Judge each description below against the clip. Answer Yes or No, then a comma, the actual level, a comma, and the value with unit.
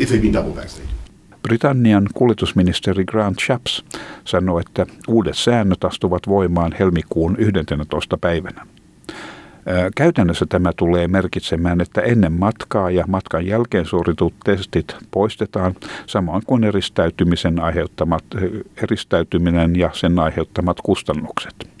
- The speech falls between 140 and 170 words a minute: No, slow, 95 wpm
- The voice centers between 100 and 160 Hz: No, very low, 90 Hz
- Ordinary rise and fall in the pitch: Yes, average, 3.1 semitones